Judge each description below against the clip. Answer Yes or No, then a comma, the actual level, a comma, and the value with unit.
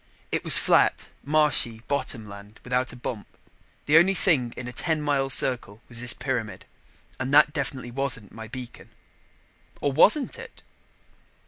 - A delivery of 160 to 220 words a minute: No, average, 150 wpm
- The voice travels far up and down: No, average, 3.8 semitones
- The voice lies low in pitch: Yes, low, 130 Hz